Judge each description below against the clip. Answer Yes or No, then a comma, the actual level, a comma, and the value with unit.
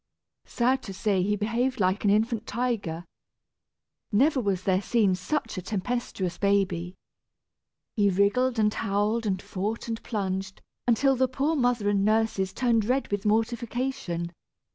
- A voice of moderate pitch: No, high, 210 Hz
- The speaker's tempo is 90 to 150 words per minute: Yes, average, 140 wpm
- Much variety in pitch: No, average, 3.8 semitones